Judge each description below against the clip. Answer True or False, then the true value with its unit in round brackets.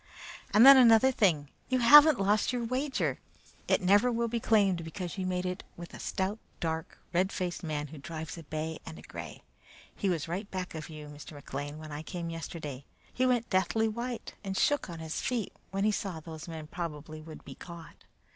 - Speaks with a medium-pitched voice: True (180 Hz)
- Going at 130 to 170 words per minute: False (205 wpm)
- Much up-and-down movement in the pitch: True (5.7 semitones)